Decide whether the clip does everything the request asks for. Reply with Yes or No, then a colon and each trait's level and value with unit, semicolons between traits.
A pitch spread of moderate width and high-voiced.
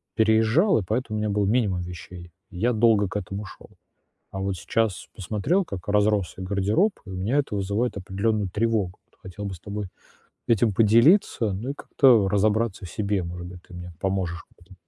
No: average, 3.0 semitones; low, 100 Hz